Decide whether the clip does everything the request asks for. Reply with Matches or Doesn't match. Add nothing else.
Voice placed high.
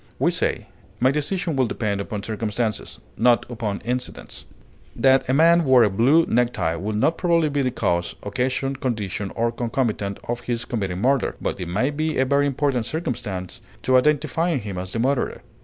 Doesn't match